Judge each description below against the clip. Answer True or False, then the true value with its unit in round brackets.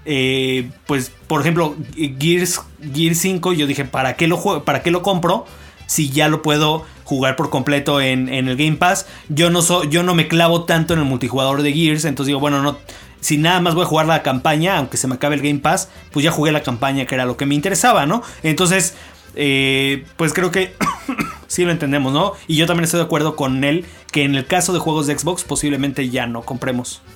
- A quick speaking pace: True (230 wpm)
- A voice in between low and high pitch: True (150 Hz)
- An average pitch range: True (3.7 semitones)